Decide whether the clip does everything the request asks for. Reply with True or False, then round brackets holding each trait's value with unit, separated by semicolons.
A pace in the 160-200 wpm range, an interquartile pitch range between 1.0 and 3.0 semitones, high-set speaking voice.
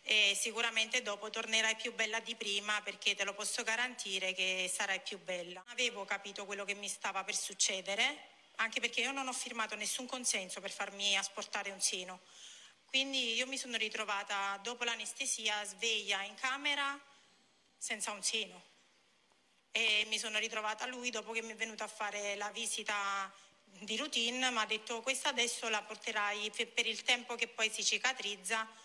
True (170 wpm; 2.6 semitones; 215 Hz)